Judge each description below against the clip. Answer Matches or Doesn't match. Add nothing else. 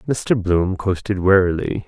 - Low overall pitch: Matches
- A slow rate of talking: Matches